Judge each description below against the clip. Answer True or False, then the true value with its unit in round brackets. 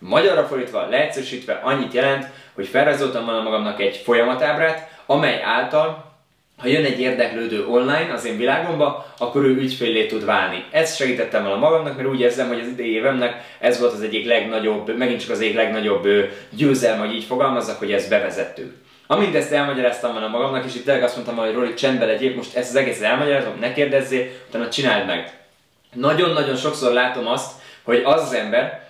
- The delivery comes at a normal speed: False (175 wpm)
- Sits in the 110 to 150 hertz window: True (125 Hz)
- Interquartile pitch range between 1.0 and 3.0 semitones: True (2.7 semitones)